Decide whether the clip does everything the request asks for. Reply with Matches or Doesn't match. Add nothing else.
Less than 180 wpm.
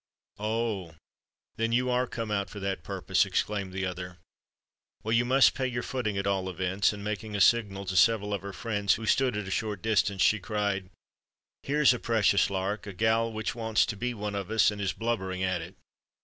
Doesn't match